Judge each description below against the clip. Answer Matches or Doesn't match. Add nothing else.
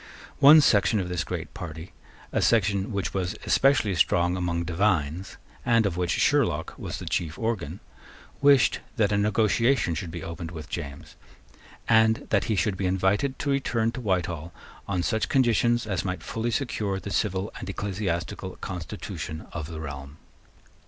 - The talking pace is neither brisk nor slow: Matches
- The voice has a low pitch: Matches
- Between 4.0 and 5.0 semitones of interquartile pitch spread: Matches